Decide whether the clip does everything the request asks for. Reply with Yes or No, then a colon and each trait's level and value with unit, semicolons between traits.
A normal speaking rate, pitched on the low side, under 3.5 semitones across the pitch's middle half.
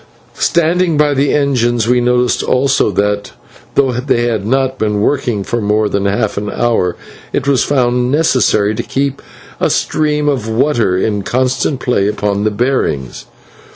No: average, 155 wpm; low, 120 Hz; average, 4.7 semitones